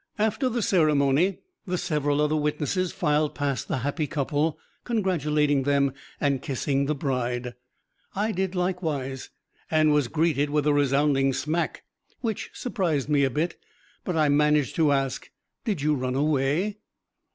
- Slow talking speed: No, average, 145 wpm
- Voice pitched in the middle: Yes, medium, 150 Hz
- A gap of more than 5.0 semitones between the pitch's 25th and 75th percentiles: No, average, 3.3 semitones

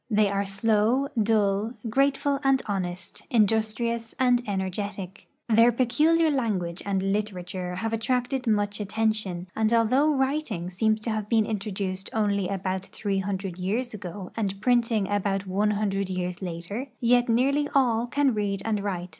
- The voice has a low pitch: No, high, 210 Hz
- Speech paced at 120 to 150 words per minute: Yes, average, 145 wpm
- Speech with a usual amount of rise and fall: Yes, average, 3.4 semitones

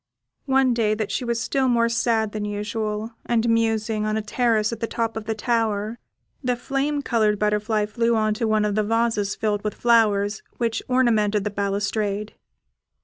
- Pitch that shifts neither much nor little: No, narrow, 1.8 semitones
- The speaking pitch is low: No, high, 220 Hz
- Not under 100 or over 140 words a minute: No, average, 180 wpm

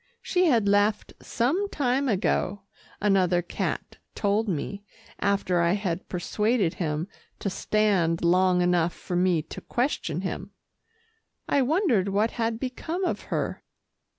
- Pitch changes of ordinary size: Yes, average, 4.6 semitones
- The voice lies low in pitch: No, high, 200 Hz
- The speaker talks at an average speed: No, slow, 130 wpm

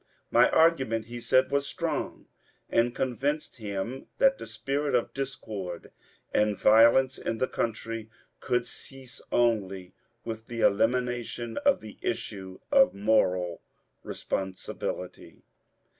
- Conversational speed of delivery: No, slow, 115 wpm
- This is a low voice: Yes, low, 115 Hz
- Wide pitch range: No, average, 3.6 semitones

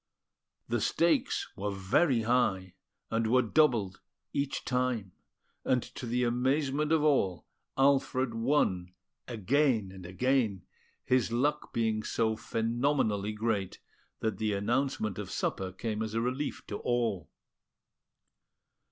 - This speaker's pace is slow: Yes, slow, 120 wpm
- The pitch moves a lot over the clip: No, average, 4.1 semitones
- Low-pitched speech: Yes, low, 115 Hz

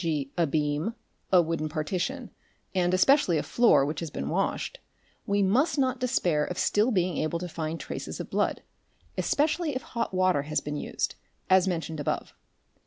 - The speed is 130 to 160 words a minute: No, average, 175 wpm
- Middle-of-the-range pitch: Yes, medium, 180 Hz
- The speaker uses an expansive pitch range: Yes, wide, 6.6 semitones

